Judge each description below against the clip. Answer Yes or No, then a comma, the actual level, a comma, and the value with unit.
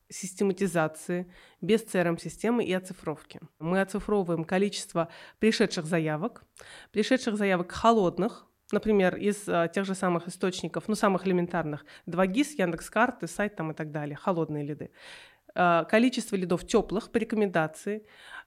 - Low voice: No, high, 190 Hz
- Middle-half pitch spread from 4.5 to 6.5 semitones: No, average, 3.9 semitones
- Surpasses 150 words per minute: No, average, 125 wpm